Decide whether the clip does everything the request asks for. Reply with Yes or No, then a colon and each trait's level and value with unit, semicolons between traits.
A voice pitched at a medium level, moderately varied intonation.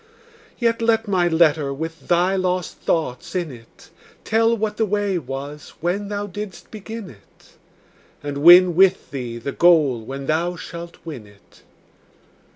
No: medium, 175 Hz; wide, 5.8 semitones